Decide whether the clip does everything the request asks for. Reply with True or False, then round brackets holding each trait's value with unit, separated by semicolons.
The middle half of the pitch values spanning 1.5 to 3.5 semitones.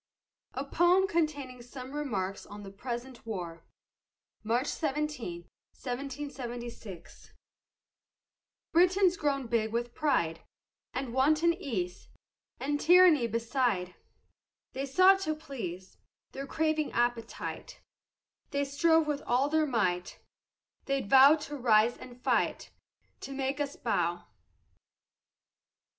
False (4.6 semitones)